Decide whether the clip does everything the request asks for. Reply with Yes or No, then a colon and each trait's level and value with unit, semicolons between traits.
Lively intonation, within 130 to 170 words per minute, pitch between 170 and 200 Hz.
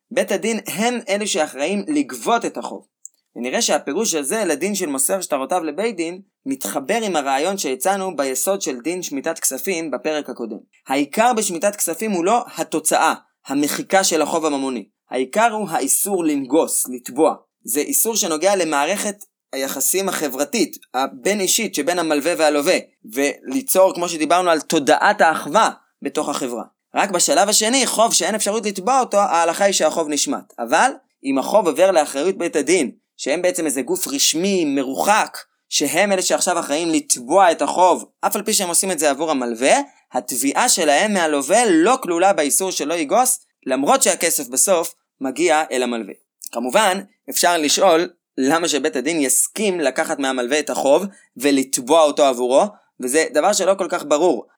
Yes: wide, 5.7 semitones; fast, 150 wpm; medium, 175 Hz